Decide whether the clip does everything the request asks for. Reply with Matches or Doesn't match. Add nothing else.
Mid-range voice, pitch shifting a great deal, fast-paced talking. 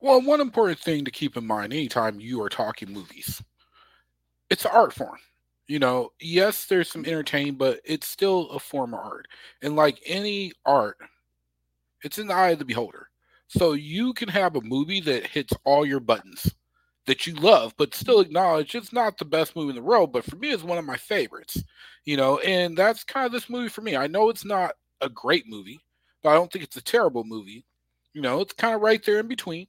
Matches